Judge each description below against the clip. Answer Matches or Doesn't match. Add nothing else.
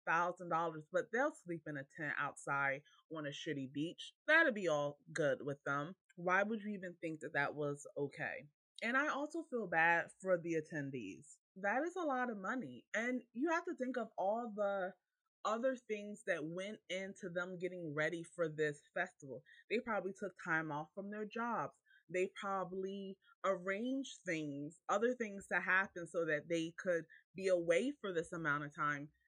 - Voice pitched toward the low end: Doesn't match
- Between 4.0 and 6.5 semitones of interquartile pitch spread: Matches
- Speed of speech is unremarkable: Matches